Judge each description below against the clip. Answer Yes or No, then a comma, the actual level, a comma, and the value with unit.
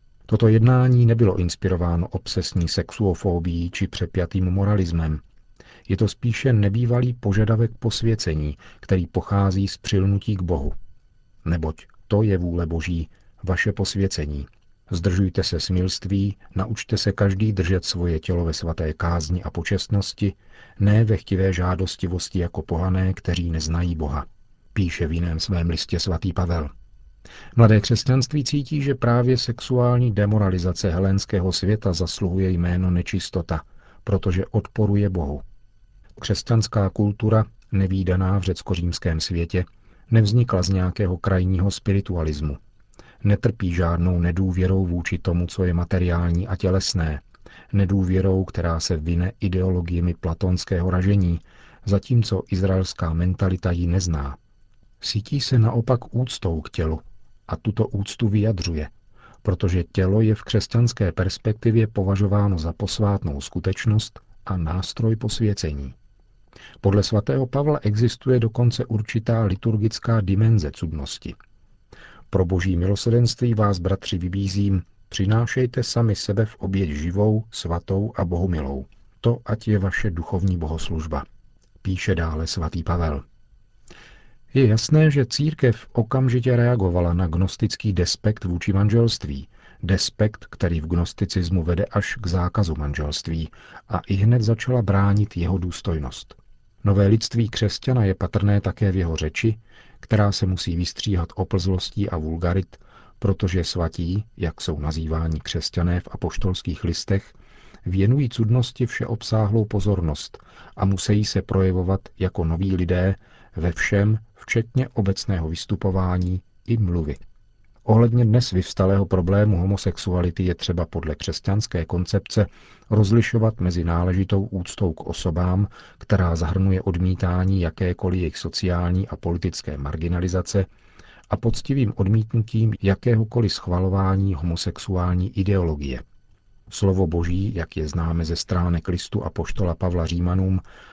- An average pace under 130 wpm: Yes, average, 120 wpm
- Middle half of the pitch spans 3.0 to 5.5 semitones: Yes, average, 3.4 semitones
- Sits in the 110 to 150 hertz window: No, very low, 95 Hz